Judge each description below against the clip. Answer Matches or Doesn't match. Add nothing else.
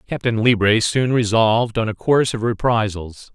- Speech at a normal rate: Matches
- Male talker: Matches